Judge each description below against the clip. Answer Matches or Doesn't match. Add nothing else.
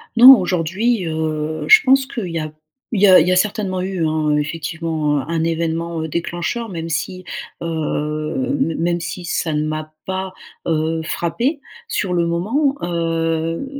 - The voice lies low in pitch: Doesn't match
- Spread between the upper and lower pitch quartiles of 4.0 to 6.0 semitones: Doesn't match